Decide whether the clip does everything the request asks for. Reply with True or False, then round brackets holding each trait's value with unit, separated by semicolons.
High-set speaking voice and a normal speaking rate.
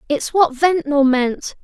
True (295 Hz; 145 wpm)